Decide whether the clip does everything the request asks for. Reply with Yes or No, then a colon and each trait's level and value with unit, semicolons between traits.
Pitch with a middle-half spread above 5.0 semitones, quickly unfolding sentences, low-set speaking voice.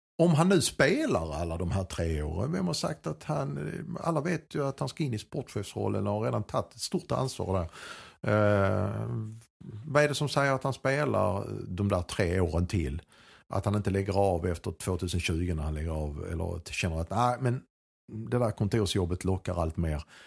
Yes: wide, 5.6 semitones; fast, 210 wpm; low, 105 Hz